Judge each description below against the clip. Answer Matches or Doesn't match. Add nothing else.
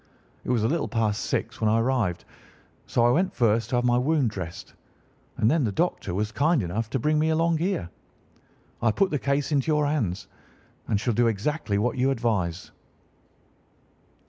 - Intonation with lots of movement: Matches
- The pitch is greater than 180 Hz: Doesn't match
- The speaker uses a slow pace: Doesn't match